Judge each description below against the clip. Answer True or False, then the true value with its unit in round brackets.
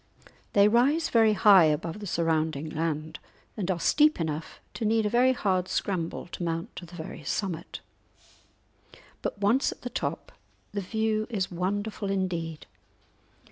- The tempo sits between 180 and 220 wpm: False (150 wpm)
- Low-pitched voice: False (190 Hz)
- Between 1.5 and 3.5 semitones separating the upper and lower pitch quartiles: False (4.7 semitones)